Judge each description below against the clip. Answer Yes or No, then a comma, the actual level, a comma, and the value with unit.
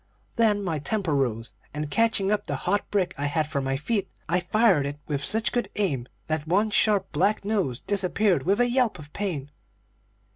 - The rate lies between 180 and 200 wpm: Yes, average, 190 wpm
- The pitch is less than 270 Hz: Yes, medium, 185 Hz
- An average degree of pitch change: No, wide, 6.0 semitones